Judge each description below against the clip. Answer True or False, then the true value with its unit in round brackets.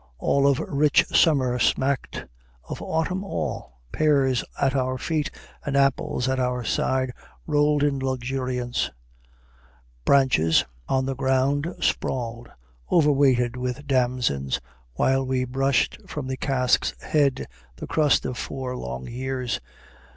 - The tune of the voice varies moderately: False (1.9 semitones)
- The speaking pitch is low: True (130 Hz)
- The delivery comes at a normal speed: False (120 wpm)